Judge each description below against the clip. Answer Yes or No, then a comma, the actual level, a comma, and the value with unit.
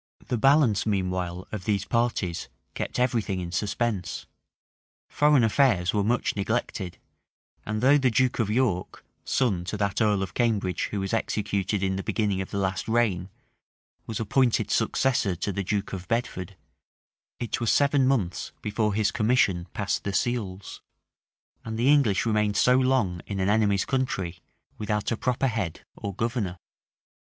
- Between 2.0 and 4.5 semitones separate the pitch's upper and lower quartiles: Yes, average, 3.8 semitones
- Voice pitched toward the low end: Yes, low, 105 Hz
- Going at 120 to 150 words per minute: No, average, 160 wpm